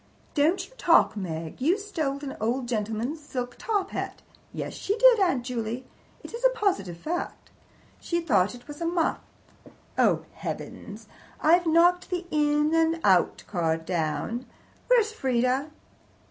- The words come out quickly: No, average, 145 wpm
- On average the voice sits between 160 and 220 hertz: No, very high, 295 Hz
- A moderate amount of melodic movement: No, wide, 7.1 semitones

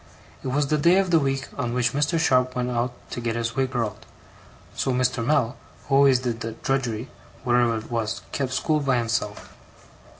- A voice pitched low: Yes, low, 125 Hz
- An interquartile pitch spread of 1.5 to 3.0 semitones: Yes, average, 2.7 semitones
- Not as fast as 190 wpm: No, average, 195 wpm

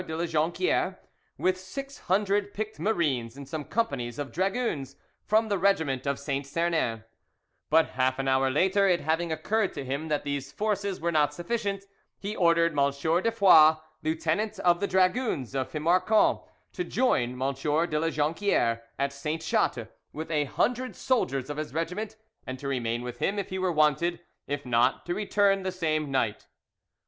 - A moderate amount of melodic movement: No, wide, 5.9 semitones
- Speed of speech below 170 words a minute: No, average, 175 wpm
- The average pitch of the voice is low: No, medium, 160 Hz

